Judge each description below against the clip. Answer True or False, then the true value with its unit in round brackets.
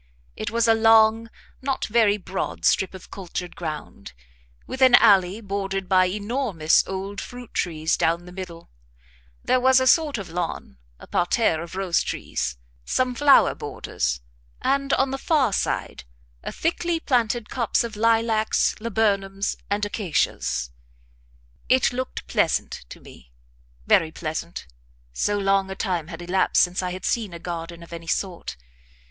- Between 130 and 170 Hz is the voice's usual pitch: False (195 Hz)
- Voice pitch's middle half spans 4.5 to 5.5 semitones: True (5.0 semitones)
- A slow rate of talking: False (150 wpm)